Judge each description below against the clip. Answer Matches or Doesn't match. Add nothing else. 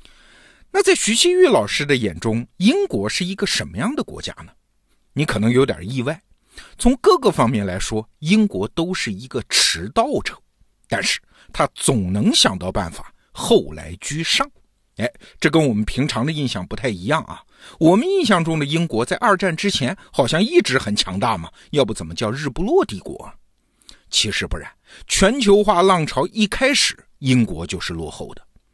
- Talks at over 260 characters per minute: Doesn't match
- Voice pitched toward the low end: Doesn't match